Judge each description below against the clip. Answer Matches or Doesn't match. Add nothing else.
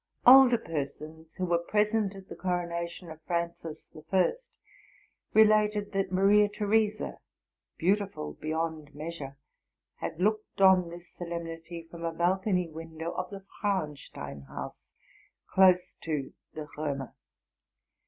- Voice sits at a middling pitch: Matches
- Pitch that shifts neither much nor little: Matches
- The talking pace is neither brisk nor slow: Doesn't match